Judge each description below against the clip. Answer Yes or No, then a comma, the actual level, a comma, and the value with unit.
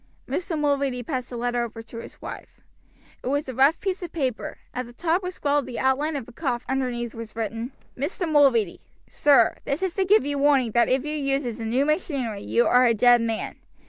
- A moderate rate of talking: No, fast, 220 wpm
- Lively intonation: No, average, 3.6 semitones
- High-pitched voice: Yes, very high, 265 Hz